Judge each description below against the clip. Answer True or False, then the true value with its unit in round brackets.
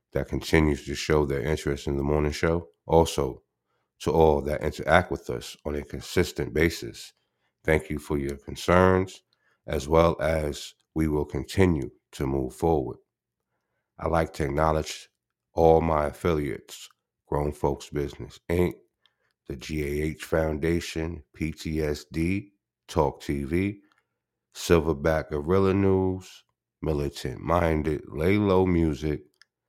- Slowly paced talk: True (120 wpm)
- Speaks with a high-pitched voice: False (80 Hz)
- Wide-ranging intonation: False (2.6 semitones)